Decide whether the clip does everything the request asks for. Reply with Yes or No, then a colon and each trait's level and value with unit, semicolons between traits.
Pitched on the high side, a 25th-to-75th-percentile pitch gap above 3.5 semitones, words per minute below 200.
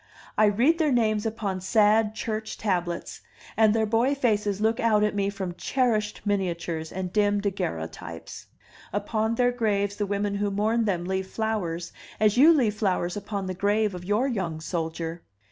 No: high, 205 Hz; average, 2.7 semitones; average, 165 wpm